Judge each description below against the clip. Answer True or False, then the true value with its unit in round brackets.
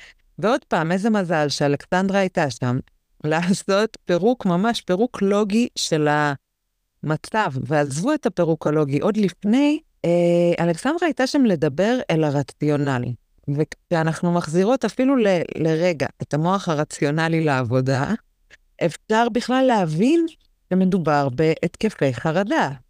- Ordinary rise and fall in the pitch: False (6.4 semitones)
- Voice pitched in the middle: True (175 Hz)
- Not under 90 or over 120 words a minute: True (105 wpm)